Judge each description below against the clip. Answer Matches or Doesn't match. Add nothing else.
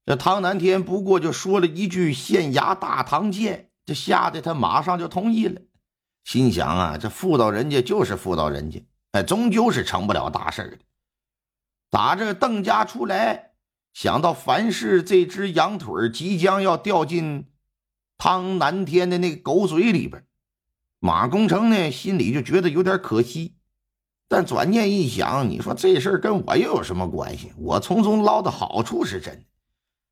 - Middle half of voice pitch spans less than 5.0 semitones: Matches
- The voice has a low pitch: Doesn't match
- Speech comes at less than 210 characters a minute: Doesn't match